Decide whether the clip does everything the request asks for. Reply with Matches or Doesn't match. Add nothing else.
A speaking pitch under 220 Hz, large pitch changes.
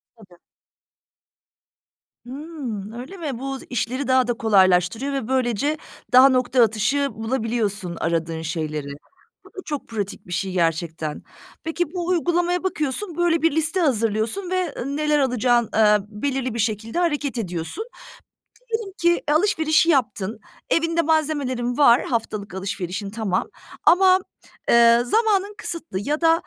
Doesn't match